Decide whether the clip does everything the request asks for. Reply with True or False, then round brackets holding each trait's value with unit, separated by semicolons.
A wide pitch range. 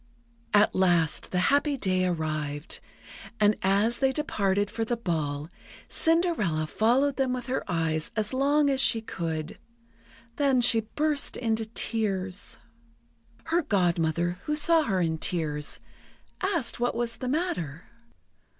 True (7.6 semitones)